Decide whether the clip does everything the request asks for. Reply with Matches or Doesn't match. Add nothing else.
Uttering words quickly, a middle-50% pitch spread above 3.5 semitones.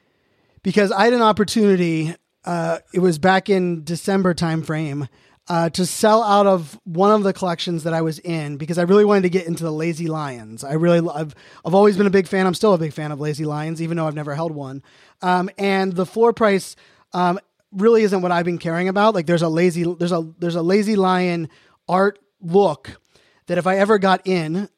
Doesn't match